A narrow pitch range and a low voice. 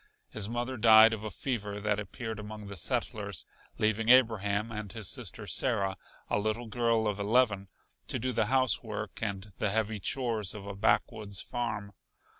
Yes: narrow, 2.3 semitones; low, 110 Hz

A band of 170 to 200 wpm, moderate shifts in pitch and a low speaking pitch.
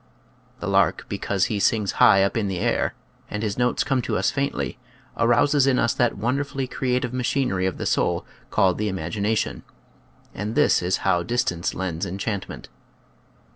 Yes: average, 175 wpm; average, 4.7 semitones; low, 110 Hz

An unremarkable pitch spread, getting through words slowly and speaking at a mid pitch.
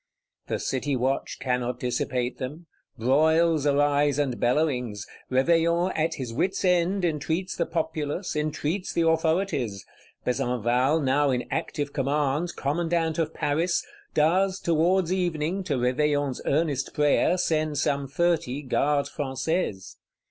Yes: average, 3.9 semitones; slow, 120 wpm; medium, 150 Hz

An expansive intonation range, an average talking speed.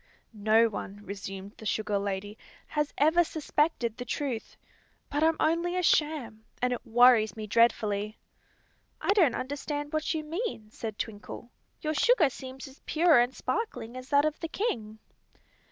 Yes: wide, 6.1 semitones; average, 155 wpm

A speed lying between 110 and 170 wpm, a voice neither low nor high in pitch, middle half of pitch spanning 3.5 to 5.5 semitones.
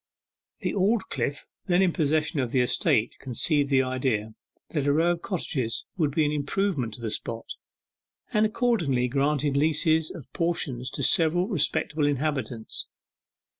Yes: average, 145 wpm; medium, 145 Hz; average, 4.5 semitones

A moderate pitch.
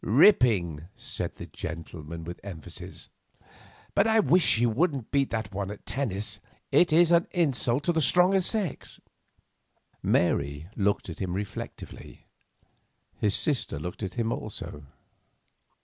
No: low, 110 Hz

